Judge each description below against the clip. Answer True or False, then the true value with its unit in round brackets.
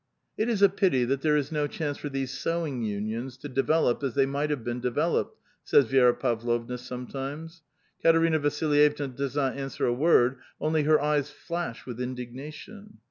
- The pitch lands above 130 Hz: True (140 Hz)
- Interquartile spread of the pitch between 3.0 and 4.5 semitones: True (3.6 semitones)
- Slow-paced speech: False (185 wpm)